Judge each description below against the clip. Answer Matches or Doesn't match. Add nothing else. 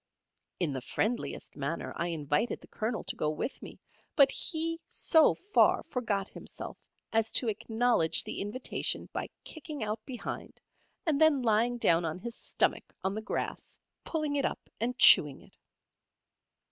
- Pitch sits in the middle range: Doesn't match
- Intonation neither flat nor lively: Doesn't match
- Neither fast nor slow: Matches